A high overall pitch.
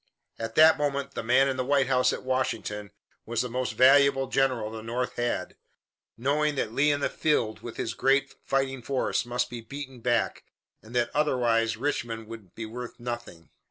No: low, 125 Hz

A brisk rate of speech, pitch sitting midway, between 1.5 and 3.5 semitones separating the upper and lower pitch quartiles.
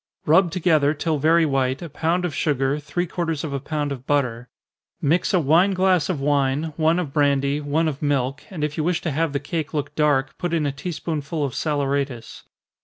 Yes: fast, 215 wpm; medium, 150 Hz; average, 2.9 semitones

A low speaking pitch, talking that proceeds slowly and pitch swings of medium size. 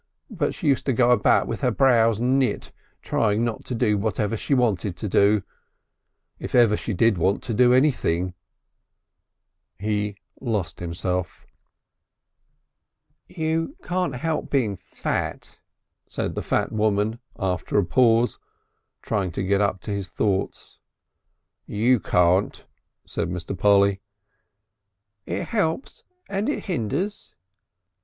Yes: low, 110 Hz; slow, 130 wpm; average, 4.3 semitones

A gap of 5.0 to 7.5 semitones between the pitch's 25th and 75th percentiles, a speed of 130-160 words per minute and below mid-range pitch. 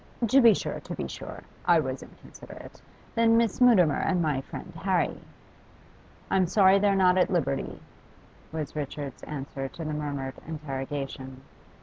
No: wide, 5.4 semitones; average, 150 wpm; medium, 160 Hz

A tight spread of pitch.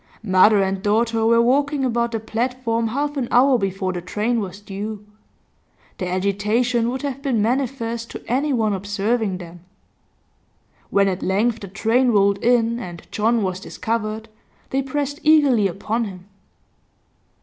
No: average, 3.6 semitones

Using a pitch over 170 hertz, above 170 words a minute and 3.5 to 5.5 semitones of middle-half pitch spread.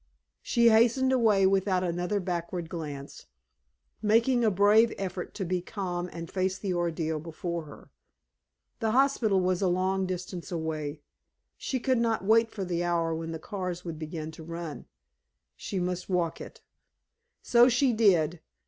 No: medium, 185 Hz; average, 155 wpm; average, 4.2 semitones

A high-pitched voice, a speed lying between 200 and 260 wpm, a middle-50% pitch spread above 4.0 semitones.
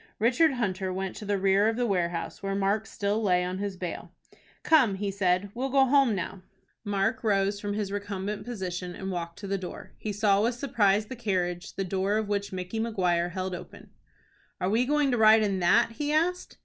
No: high, 200 Hz; fast, 205 wpm; average, 3.0 semitones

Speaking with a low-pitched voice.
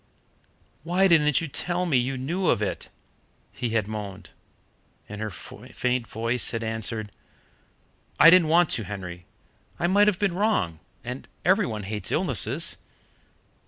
Yes: low, 125 Hz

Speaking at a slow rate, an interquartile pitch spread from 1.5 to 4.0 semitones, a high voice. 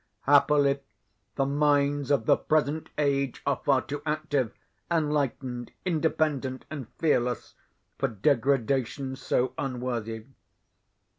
No: slow, 100 wpm; narrow, 2.4 semitones; medium, 140 Hz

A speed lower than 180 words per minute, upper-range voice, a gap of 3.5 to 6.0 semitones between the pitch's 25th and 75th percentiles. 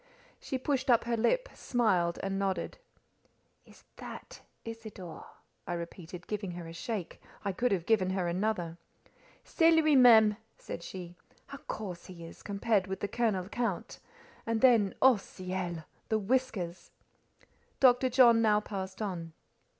Yes: average, 140 wpm; high, 205 Hz; average, 4.6 semitones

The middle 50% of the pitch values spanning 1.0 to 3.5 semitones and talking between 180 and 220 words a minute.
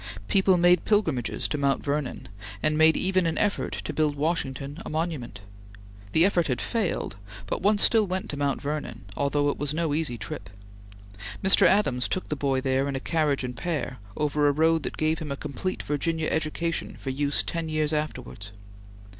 Yes: average, 3.2 semitones; average, 185 wpm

